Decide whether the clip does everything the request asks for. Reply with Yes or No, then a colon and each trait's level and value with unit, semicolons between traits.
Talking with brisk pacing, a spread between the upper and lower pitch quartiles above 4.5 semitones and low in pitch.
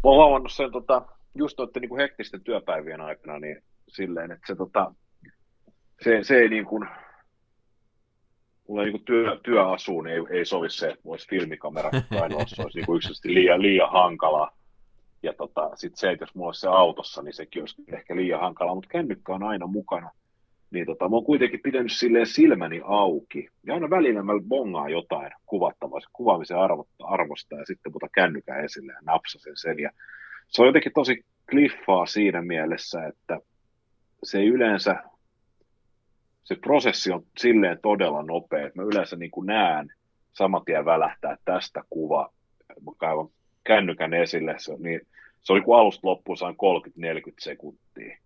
Yes: fast, 170 wpm; average, 5.2 semitones; low, 115 Hz